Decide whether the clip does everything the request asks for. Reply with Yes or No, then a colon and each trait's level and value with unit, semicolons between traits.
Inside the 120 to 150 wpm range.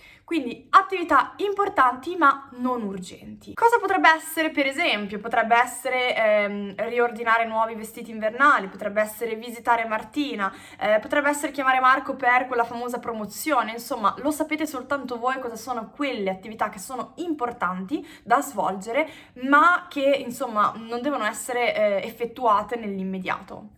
Yes: average, 135 wpm